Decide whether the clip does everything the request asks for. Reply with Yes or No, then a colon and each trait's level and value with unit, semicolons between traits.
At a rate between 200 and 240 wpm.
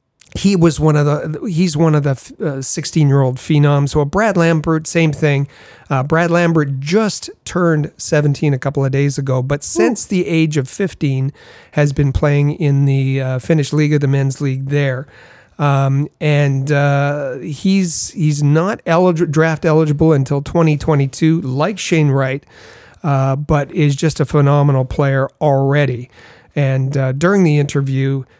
No: average, 165 wpm